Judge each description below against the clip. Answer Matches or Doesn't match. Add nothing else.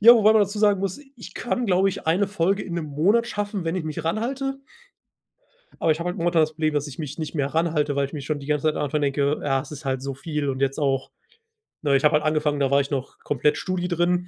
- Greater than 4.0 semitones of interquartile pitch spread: Matches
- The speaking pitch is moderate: Matches